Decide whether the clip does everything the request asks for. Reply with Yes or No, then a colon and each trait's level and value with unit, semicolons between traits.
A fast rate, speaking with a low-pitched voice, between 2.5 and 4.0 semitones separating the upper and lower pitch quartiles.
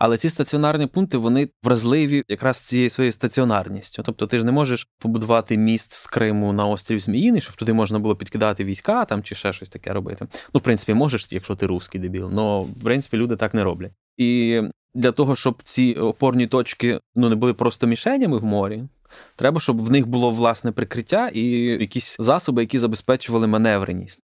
Yes: fast, 185 wpm; low, 115 Hz; average, 2.9 semitones